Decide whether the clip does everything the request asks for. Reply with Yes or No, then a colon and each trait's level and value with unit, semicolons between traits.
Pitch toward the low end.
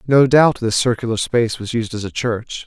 Yes: low, 115 Hz